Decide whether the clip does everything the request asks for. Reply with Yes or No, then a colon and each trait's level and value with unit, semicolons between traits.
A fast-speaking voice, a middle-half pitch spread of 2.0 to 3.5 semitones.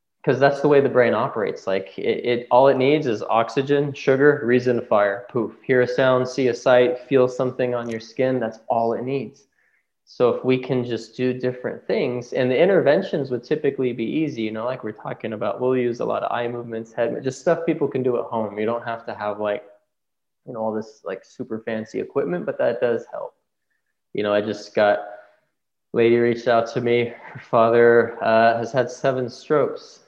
Yes: fast, 210 wpm; narrow, 2.6 semitones